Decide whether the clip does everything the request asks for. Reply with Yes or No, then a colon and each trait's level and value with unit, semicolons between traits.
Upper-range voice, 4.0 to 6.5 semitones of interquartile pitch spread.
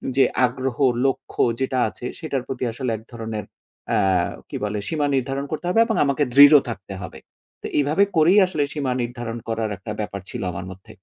No: low, 130 Hz; average, 4.4 semitones